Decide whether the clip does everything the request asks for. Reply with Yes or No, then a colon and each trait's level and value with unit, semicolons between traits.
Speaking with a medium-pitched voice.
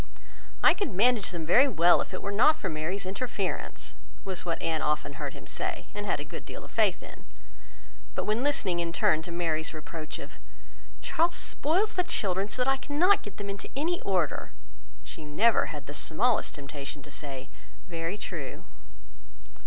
Yes: medium, 180 Hz